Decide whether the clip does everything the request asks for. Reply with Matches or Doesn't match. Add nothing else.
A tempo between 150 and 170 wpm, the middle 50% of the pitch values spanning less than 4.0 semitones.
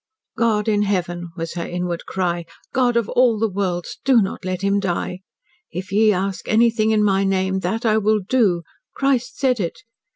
Doesn't match